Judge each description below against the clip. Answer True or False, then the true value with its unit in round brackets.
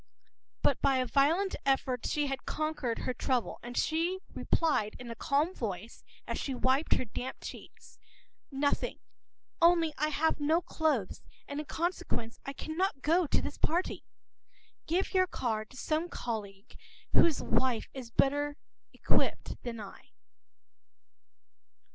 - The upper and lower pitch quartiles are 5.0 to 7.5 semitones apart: False (4.6 semitones)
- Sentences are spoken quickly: False (145 wpm)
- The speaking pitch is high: True (280 Hz)